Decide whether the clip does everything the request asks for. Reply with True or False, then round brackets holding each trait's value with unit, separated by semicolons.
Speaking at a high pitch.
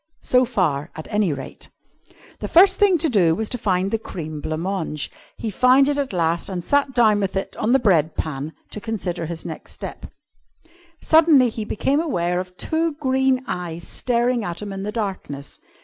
True (205 Hz)